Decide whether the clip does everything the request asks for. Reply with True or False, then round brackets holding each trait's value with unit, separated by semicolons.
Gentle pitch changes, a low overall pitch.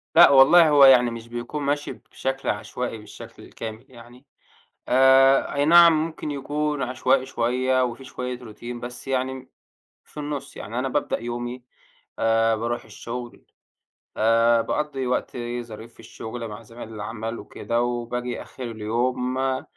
True (2.3 semitones; 125 Hz)